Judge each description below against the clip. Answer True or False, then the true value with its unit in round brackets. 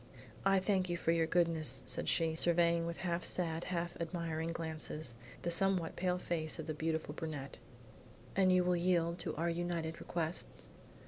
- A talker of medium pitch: True (170 Hz)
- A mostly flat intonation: True (1.5 semitones)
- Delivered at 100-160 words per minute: False (170 wpm)